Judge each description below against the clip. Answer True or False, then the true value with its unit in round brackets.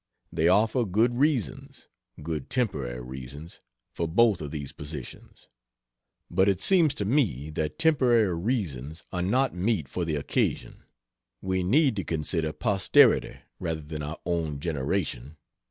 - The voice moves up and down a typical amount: False (6.7 semitones)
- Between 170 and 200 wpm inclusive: False (140 wpm)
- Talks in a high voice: False (85 Hz)